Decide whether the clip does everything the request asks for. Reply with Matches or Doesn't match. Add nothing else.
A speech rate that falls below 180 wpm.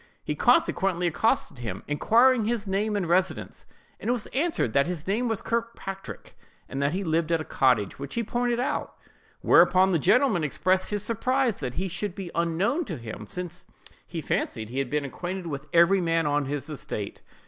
Doesn't match